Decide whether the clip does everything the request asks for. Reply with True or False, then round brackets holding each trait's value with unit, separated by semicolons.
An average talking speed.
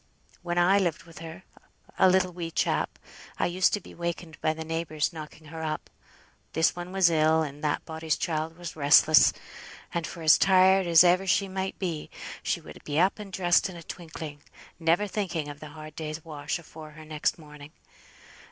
True (190 wpm)